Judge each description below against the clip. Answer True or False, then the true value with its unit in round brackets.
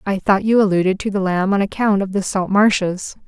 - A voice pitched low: False (195 Hz)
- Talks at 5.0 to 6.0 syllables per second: True (5.5 syllables/s)